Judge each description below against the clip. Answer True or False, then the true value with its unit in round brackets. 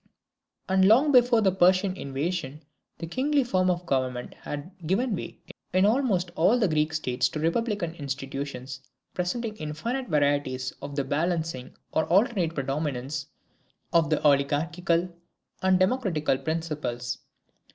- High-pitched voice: False (165 Hz)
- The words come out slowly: True (130 wpm)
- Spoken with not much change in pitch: False (5.0 semitones)